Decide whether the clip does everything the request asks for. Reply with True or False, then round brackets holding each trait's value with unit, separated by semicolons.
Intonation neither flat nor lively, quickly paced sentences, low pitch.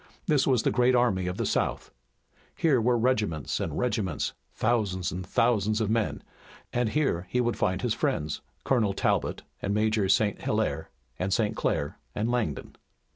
False (4.3 semitones; 165 wpm; 110 Hz)